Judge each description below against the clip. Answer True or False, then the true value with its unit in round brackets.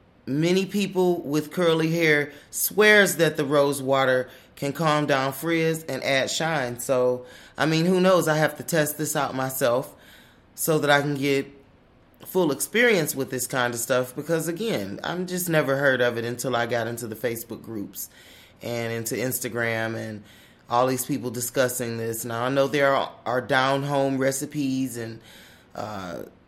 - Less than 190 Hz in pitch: True (135 Hz)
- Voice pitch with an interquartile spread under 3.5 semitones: False (3.8 semitones)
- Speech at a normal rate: True (170 wpm)